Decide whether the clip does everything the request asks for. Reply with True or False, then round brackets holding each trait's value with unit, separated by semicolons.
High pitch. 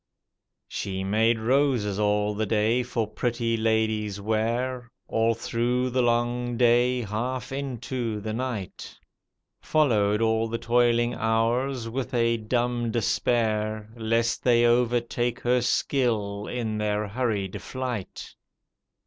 False (115 Hz)